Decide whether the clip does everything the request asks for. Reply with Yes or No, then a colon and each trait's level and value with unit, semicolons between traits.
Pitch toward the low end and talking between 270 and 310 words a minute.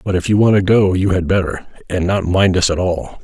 Yes: very low, 90 Hz; fast, 280 wpm